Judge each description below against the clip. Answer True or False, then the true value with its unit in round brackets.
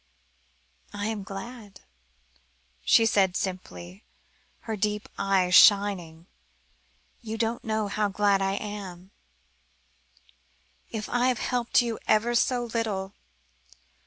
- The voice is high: True (205 Hz)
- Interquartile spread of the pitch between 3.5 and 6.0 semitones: False (2.8 semitones)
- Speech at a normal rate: False (105 wpm)